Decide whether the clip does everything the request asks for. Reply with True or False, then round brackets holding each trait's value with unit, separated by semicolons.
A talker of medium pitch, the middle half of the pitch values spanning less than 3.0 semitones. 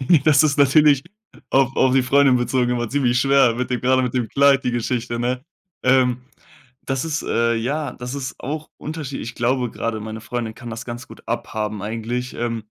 False (125 Hz; 2.4 semitones)